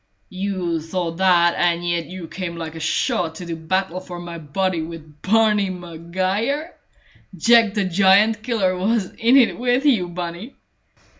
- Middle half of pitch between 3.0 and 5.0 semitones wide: Yes, average, 3.5 semitones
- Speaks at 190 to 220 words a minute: No, average, 155 wpm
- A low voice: No, medium, 185 Hz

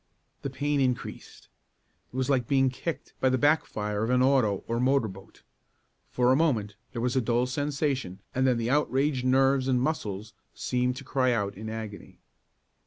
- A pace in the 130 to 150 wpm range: No, average, 180 wpm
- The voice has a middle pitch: No, low, 130 Hz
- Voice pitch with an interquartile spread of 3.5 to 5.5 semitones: No, average, 2.9 semitones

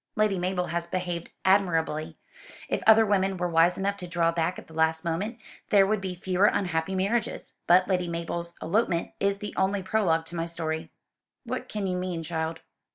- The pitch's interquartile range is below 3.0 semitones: Yes, narrow, 2.6 semitones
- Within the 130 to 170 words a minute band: No, average, 185 wpm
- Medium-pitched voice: Yes, medium, 180 Hz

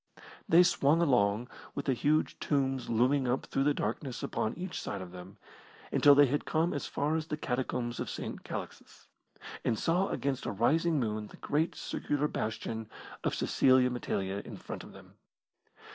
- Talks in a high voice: No, low, 135 Hz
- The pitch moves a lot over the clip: No, average, 4.8 semitones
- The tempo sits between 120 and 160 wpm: No, average, 175 wpm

